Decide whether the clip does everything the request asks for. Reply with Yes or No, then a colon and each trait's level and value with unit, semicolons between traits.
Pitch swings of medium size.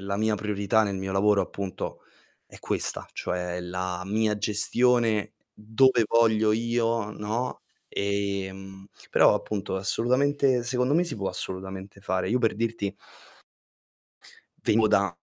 Yes: average, 3.1 semitones